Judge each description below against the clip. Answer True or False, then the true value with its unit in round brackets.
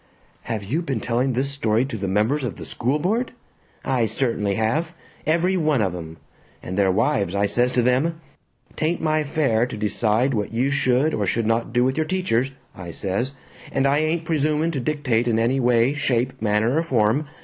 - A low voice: True (125 Hz)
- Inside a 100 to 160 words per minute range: False (195 wpm)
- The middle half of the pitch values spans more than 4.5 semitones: True (5.2 semitones)